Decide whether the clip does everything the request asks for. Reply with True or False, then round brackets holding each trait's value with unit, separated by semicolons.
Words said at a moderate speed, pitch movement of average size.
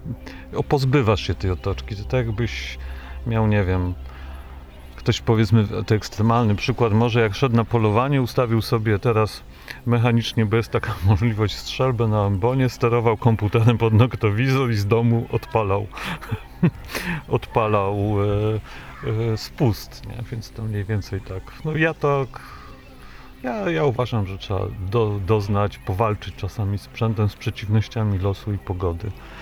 True (140 wpm; 3.0 semitones)